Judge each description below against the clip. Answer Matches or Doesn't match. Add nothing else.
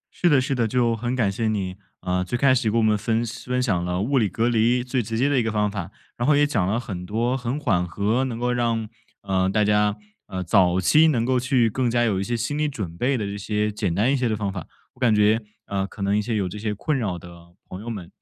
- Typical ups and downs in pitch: Matches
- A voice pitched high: Doesn't match